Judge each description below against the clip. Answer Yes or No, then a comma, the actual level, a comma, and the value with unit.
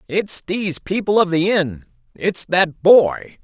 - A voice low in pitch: No, medium, 175 Hz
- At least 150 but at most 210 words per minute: No, average, 140 wpm